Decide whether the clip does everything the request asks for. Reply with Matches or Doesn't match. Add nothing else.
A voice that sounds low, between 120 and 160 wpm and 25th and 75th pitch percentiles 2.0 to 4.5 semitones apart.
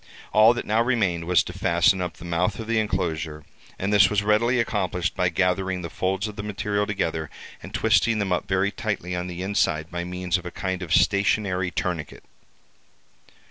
Doesn't match